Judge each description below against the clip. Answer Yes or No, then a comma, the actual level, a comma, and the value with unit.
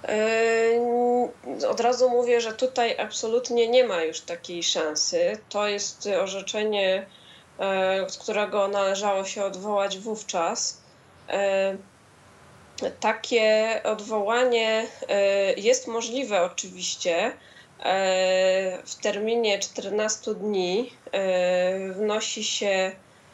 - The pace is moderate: No, slow, 80 wpm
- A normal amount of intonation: Yes, average, 3.0 semitones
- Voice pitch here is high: Yes, high, 210 Hz